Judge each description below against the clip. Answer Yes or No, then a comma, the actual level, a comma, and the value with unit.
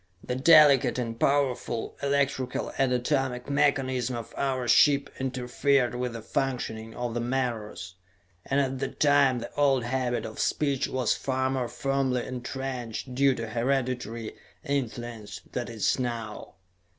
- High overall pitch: No, low, 125 Hz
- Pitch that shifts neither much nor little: No, narrow, 2.3 semitones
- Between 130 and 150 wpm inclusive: Yes, average, 140 wpm